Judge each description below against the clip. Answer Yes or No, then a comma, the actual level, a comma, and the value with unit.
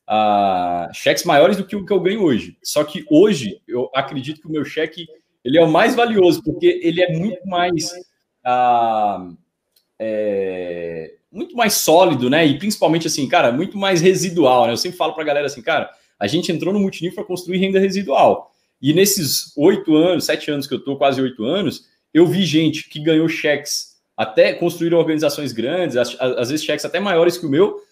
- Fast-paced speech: Yes, fast, 190 wpm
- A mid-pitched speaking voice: Yes, medium, 165 Hz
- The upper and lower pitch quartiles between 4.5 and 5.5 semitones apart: Yes, average, 5.1 semitones